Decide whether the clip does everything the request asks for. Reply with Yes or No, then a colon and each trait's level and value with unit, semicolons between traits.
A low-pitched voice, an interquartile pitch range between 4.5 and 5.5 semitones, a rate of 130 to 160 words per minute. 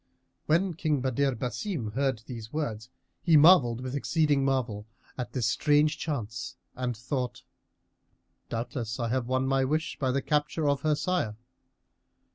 No: low, 130 Hz; average, 3.9 semitones; average, 145 wpm